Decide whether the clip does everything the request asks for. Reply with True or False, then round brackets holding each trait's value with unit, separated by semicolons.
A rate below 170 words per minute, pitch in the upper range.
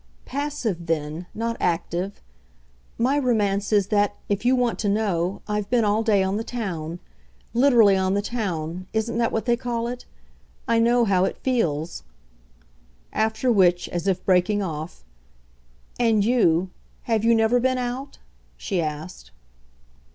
True (150 wpm; 210 Hz)